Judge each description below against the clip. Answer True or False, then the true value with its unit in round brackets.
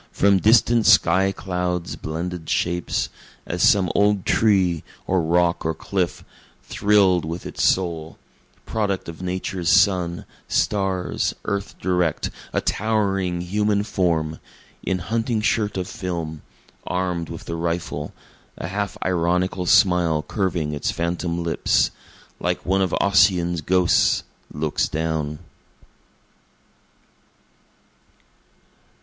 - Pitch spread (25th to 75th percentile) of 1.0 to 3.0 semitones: True (2.4 semitones)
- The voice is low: True (90 Hz)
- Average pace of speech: False (110 wpm)